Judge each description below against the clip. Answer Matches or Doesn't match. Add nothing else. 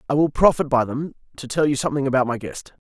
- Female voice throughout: Doesn't match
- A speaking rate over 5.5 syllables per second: Matches